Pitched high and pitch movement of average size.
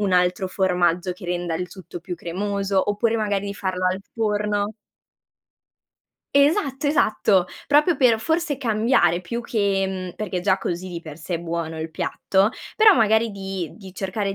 Yes: high, 195 Hz; average, 3.5 semitones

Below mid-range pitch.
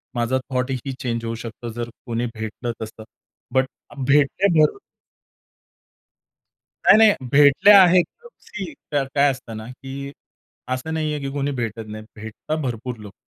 Yes: low, 130 Hz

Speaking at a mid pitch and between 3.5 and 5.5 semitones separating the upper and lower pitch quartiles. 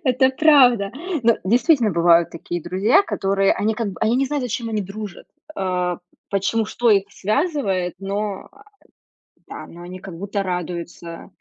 No: high, 200 Hz; average, 4.5 semitones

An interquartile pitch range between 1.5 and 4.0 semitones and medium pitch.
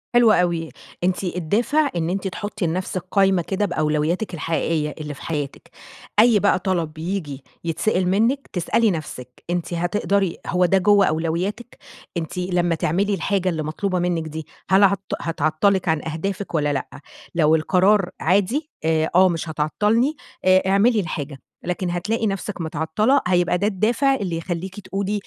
Yes: average, 3.7 semitones; medium, 180 Hz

